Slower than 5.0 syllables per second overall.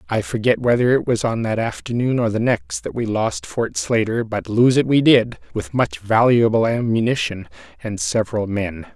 Yes: 4.8 syllables/s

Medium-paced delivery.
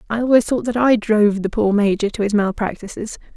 No: fast, 215 wpm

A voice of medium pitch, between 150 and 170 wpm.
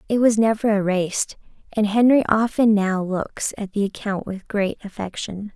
No: high, 205 Hz; average, 160 wpm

